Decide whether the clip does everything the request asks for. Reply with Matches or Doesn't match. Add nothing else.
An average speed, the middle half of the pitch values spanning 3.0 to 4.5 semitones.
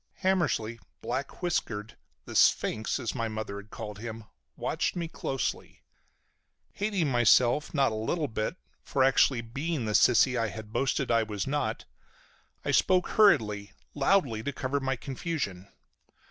Doesn't match